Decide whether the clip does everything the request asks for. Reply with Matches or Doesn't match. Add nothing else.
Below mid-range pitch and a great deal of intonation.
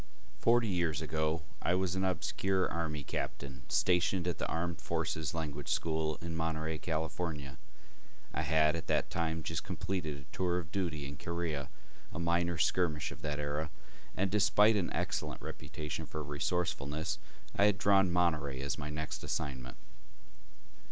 Doesn't match